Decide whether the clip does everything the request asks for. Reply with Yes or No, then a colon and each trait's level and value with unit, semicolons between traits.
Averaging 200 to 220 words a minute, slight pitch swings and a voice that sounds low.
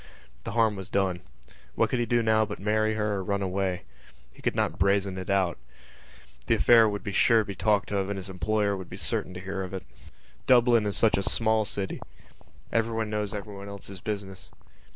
Yes: fast, 205 wpm; narrow, 2.1 semitones; low, 100 Hz